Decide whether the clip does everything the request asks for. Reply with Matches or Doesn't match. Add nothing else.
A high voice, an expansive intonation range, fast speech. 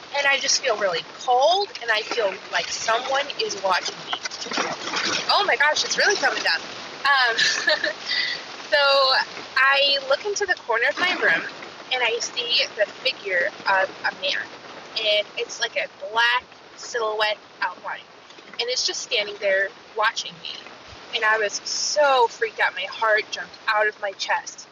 Doesn't match